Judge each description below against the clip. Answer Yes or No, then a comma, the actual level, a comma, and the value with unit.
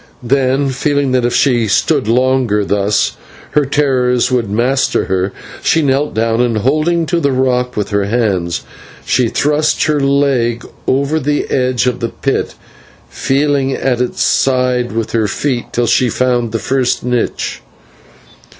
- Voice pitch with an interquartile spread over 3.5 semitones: No, average, 2.9 semitones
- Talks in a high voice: No, low, 125 Hz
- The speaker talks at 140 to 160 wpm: Yes, average, 150 wpm